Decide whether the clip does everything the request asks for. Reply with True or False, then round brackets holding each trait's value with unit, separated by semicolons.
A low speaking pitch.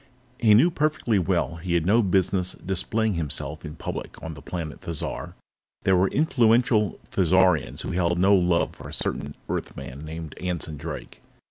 True (90 Hz)